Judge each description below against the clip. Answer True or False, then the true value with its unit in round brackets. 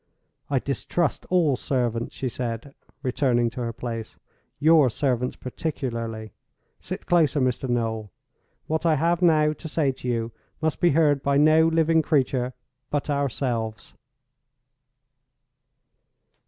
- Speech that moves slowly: True (120 wpm)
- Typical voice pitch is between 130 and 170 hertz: True (135 Hz)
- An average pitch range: True (4.6 semitones)